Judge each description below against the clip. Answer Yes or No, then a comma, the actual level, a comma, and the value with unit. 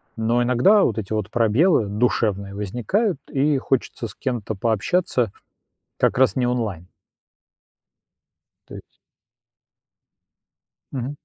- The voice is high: No, low, 120 Hz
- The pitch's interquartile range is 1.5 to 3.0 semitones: No, average, 3.9 semitones